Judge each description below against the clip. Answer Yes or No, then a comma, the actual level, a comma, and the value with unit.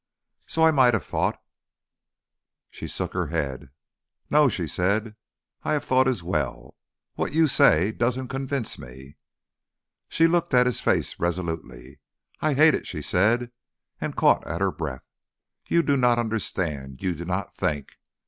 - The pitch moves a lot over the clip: Yes, wide, 8.0 semitones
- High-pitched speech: No, low, 105 Hz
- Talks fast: No, average, 160 wpm